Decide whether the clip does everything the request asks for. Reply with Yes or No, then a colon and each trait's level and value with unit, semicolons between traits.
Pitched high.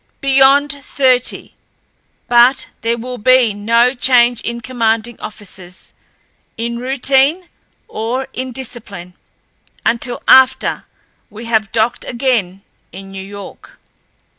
Yes: high, 240 Hz